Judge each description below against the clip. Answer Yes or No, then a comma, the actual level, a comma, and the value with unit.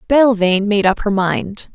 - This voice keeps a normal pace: Yes, average, 170 wpm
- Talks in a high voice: Yes, high, 205 Hz